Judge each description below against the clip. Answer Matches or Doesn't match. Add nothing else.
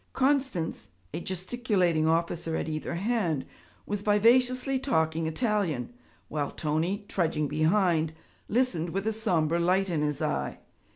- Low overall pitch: Doesn't match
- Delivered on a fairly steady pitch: Doesn't match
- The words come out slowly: Matches